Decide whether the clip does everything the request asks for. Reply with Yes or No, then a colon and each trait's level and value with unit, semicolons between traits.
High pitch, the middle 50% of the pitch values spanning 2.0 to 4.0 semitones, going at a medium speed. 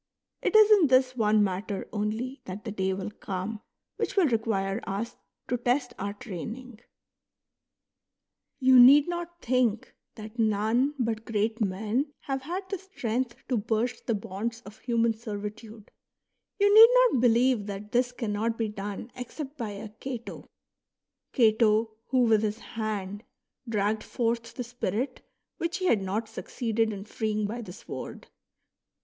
Yes: high, 225 Hz; average, 3.2 semitones; average, 150 wpm